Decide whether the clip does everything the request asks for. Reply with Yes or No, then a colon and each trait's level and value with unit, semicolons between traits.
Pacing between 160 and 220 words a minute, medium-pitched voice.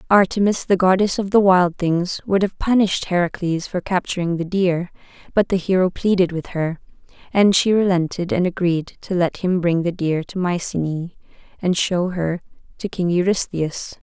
Yes: average, 170 wpm; medium, 180 Hz